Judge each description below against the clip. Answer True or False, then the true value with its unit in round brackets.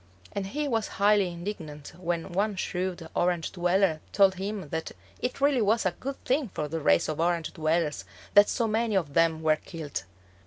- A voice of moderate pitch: True (180 Hz)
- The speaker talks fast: False (185 wpm)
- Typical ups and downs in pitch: True (4.3 semitones)